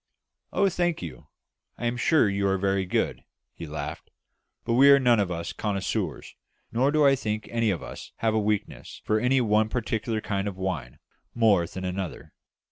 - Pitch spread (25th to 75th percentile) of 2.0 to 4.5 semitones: Yes, average, 4.0 semitones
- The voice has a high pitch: No, low, 105 Hz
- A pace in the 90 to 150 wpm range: No, average, 185 wpm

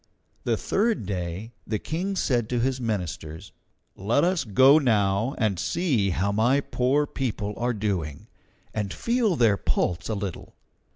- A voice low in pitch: Yes, low, 110 Hz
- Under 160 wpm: Yes, average, 150 wpm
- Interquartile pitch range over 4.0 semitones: Yes, wide, 5.6 semitones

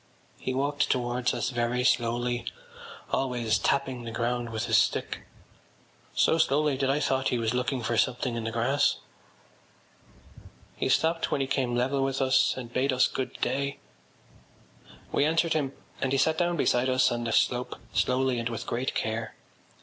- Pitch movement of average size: No, narrow, 2.2 semitones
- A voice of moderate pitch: No, low, 130 Hz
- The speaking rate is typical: Yes, average, 170 wpm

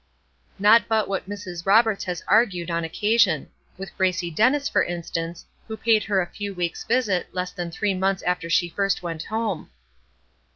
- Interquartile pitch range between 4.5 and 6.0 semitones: No, average, 3.6 semitones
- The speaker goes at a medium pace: Yes, average, 170 wpm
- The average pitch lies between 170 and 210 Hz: Yes, high, 190 Hz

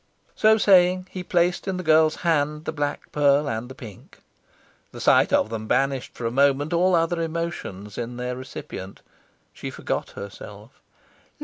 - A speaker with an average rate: Yes, average, 165 wpm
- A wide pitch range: Yes, wide, 5.7 semitones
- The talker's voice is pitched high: No, medium, 145 Hz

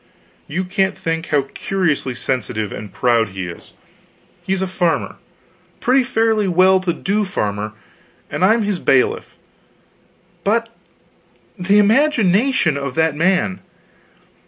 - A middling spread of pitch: No, wide, 6.6 semitones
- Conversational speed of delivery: No, slow, 120 wpm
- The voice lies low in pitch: No, medium, 185 Hz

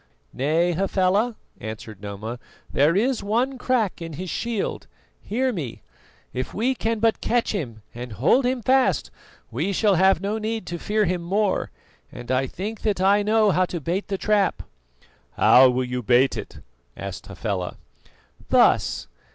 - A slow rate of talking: No, average, 160 wpm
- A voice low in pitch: No, high, 190 Hz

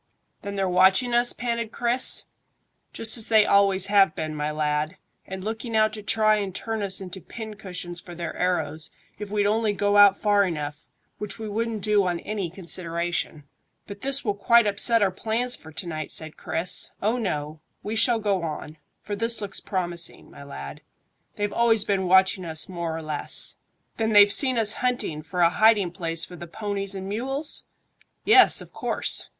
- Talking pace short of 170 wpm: No, average, 185 wpm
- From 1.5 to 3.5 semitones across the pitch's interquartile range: No, average, 4.1 semitones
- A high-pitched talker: Yes, high, 200 Hz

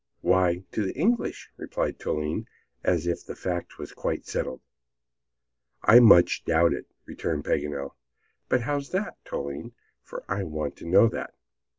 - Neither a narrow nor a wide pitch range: No, wide, 7.1 semitones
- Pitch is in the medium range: No, very low, 90 Hz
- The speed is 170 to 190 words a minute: No, average, 150 wpm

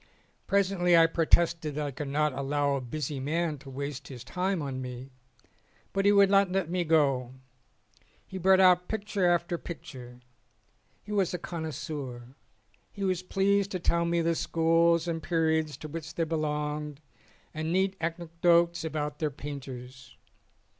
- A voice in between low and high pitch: Yes, medium, 160 Hz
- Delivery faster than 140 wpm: Yes, average, 155 wpm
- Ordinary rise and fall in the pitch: Yes, average, 3.5 semitones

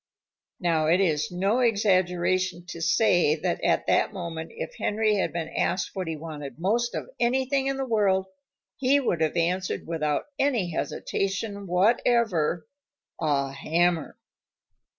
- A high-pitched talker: No, medium, 180 Hz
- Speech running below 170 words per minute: Yes, average, 140 wpm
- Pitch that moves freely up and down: No, average, 4.6 semitones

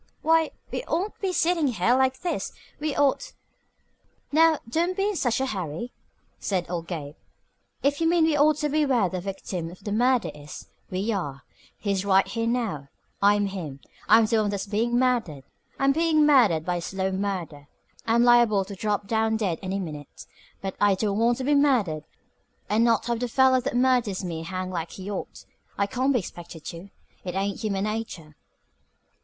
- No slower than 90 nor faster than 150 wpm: No, average, 190 wpm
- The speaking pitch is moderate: No, high, 215 Hz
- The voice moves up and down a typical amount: No, wide, 5.9 semitones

